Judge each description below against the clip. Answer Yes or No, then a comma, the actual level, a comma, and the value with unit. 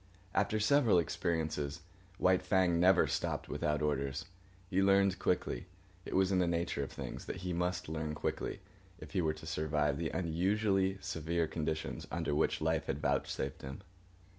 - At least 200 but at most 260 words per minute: No, average, 165 wpm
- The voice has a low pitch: Yes, very low, 85 Hz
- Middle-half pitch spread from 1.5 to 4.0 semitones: Yes, average, 3.1 semitones